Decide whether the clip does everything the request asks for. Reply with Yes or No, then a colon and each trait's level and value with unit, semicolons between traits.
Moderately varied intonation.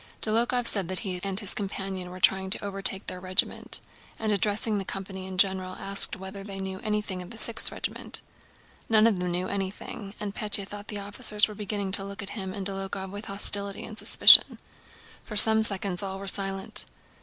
No: narrow, 1.5 semitones